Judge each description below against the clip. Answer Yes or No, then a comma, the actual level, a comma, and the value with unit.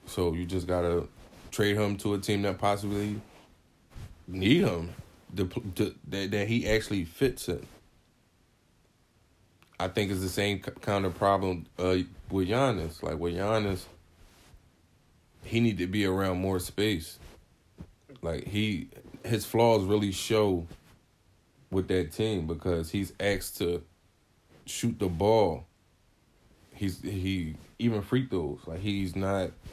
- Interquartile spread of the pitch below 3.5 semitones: Yes, average, 2.8 semitones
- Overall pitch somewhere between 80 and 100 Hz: Yes, very low, 95 Hz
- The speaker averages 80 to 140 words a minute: Yes, slow, 135 wpm